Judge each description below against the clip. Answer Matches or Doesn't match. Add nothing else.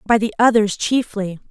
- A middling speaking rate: Matches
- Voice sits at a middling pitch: Doesn't match